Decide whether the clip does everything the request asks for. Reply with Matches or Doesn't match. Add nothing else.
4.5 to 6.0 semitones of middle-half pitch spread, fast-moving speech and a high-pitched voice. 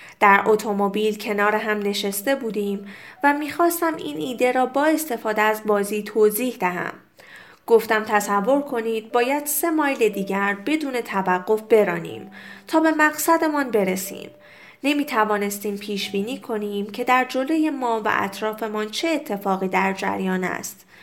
Doesn't match